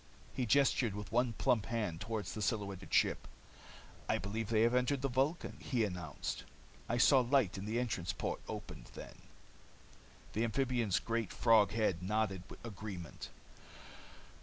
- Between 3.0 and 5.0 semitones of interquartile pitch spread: Yes, average, 3.4 semitones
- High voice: No, low, 110 Hz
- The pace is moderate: Yes, average, 145 wpm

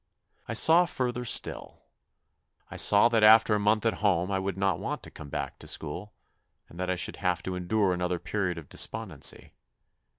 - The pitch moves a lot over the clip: No, average, 3.4 semitones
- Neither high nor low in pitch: No, low, 100 Hz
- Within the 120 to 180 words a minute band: No, average, 190 wpm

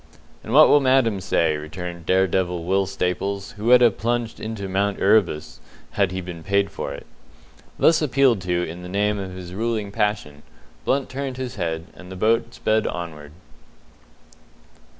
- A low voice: Yes, low, 100 Hz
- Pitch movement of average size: Yes, average, 4.1 semitones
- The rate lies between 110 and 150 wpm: No, average, 170 wpm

